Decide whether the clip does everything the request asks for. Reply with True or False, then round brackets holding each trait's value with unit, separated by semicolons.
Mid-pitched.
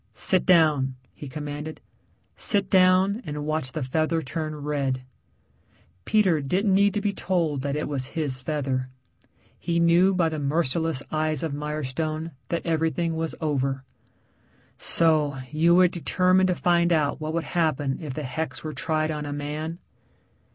True (155 Hz)